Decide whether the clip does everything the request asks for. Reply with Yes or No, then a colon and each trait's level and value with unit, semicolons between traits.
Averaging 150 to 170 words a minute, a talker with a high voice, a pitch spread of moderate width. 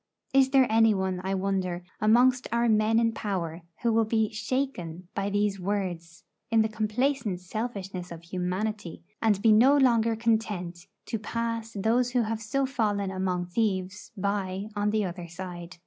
Yes: average, 165 wpm; high, 210 Hz; average, 3.5 semitones